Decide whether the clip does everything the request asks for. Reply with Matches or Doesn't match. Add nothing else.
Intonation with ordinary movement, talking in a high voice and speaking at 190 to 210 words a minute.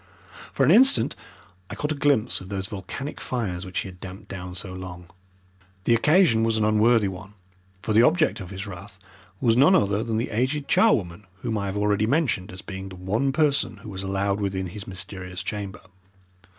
Doesn't match